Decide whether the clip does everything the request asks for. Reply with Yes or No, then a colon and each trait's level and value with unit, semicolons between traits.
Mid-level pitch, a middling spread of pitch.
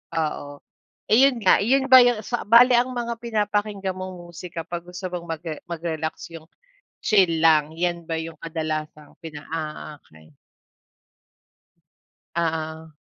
Yes: medium, 170 Hz; average, 4.7 semitones